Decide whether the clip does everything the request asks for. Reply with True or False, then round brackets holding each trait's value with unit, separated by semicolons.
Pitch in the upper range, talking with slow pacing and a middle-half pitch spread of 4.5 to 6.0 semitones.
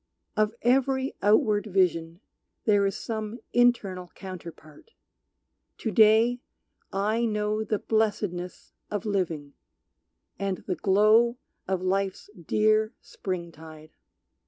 False (205 Hz; 105 wpm; 3.0 semitones)